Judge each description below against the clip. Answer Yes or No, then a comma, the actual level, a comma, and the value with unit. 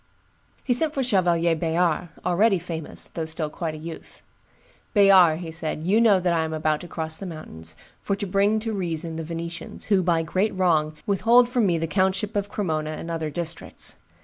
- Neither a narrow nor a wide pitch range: Yes, average, 3.5 semitones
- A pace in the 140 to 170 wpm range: No, average, 195 wpm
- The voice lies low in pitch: No, medium, 175 Hz